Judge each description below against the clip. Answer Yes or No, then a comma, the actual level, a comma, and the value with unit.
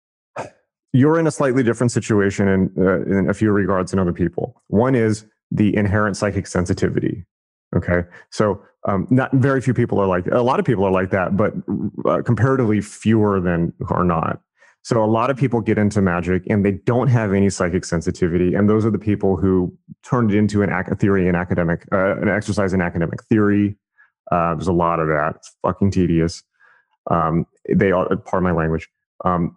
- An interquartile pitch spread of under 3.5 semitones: Yes, average, 3.1 semitones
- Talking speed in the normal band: Yes, average, 195 wpm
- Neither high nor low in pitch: No, low, 100 Hz